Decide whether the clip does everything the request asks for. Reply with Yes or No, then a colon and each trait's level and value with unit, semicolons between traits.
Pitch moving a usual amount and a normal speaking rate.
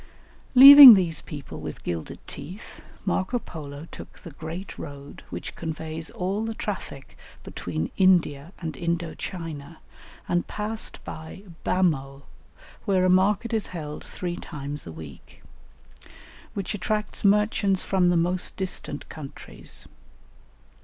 No: average, 4.6 semitones; slow, 125 wpm